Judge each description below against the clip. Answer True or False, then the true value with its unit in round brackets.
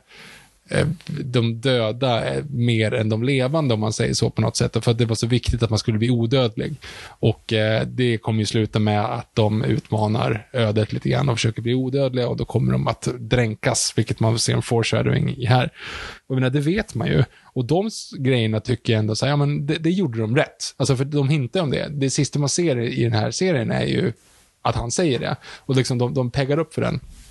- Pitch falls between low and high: False (125 Hz)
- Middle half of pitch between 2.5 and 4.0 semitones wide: True (3.6 semitones)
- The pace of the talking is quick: True (225 wpm)